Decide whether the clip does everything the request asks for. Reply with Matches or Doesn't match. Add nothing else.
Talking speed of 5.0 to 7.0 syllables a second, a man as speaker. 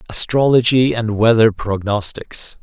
Doesn't match